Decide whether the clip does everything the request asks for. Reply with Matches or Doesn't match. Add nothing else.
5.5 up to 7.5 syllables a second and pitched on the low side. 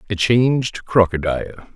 Matches